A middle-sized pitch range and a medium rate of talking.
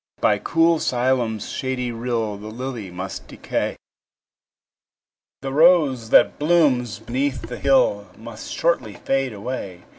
No: average, 3.8 semitones; slow, 120 wpm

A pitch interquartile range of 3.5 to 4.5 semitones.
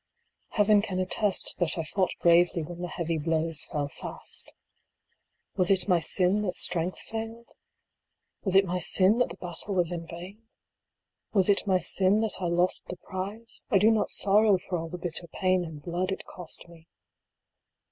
No: average, 2.7 semitones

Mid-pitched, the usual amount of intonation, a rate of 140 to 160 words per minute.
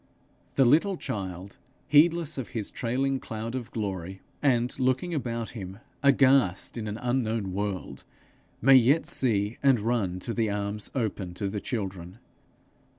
No: low, 115 Hz; average, 4.7 semitones; average, 145 wpm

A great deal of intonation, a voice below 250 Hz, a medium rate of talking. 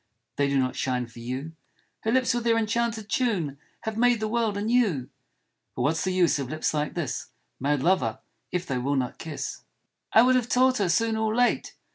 No: wide, 8.5 semitones; medium, 185 Hz; fast, 215 wpm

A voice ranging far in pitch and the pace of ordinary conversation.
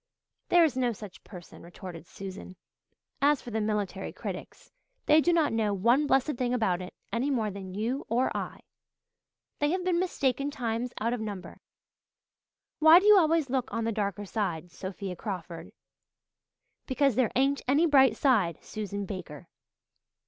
Yes: wide, 6.1 semitones; average, 160 wpm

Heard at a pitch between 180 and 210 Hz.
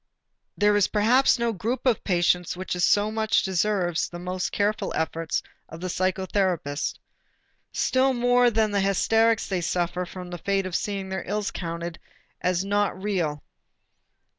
Yes: high, 190 Hz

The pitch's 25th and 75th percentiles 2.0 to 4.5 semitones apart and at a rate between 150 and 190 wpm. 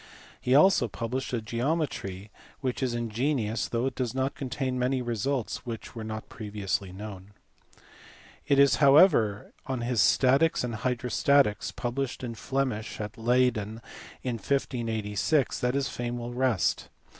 No: average, 3.3 semitones; average, 140 wpm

